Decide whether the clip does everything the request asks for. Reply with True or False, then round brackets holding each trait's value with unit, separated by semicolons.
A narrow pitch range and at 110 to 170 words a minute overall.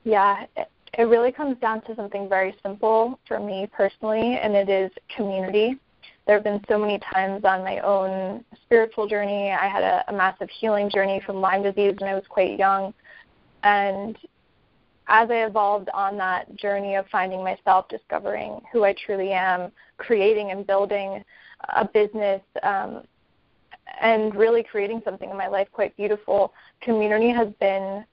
True (2.2 semitones; 160 wpm)